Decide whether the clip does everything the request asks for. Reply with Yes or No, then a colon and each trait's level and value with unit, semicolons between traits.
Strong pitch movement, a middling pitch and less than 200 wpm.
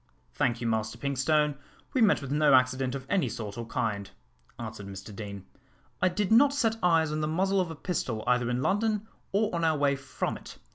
No: wide, 7.7 semitones; medium, 145 Hz; fast, 205 wpm